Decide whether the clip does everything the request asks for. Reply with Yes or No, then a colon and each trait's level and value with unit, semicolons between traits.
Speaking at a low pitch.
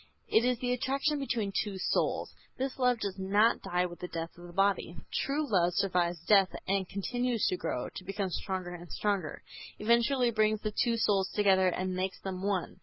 No: high, 195 Hz